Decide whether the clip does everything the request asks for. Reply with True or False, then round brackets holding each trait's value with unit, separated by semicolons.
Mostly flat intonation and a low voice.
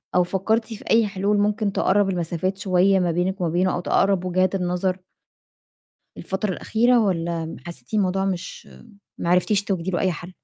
False (2.1 semitones; 185 Hz)